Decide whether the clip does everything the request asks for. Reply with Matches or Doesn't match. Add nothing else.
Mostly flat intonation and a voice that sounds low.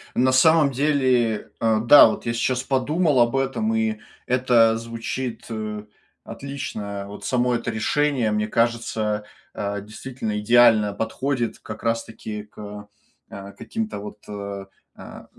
Doesn't match